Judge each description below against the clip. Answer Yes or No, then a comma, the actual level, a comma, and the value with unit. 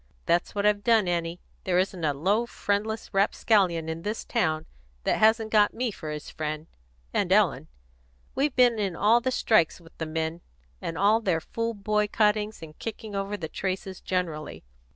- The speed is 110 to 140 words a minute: No, average, 175 wpm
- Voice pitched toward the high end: Yes, high, 195 Hz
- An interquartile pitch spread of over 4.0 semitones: Yes, average, 4.7 semitones